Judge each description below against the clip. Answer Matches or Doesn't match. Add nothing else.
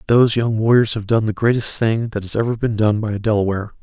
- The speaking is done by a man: Matches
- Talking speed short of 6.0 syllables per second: Doesn't match